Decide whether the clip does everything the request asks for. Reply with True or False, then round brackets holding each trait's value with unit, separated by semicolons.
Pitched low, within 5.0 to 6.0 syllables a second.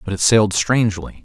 False (105 Hz; 6.3 syllables/s)